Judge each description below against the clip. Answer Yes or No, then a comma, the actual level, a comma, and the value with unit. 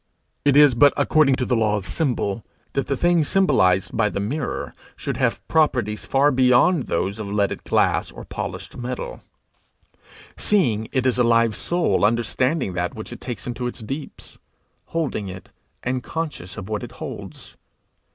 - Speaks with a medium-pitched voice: No, low, 125 Hz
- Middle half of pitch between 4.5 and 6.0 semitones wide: Yes, average, 5.0 semitones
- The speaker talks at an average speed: Yes, average, 165 wpm